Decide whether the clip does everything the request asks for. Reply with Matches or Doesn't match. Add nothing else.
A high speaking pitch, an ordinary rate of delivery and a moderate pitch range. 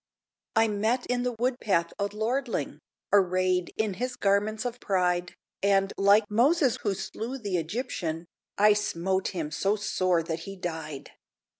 Matches